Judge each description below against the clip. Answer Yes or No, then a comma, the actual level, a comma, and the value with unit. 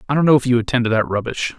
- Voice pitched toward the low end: Yes, low, 125 Hz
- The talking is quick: Yes, fast, 340 wpm